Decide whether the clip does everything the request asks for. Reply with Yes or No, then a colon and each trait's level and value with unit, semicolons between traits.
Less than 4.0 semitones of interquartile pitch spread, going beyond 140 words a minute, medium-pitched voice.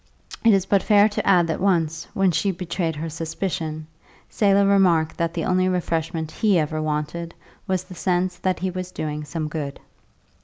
Yes: average, 2.9 semitones; average, 180 wpm; medium, 175 Hz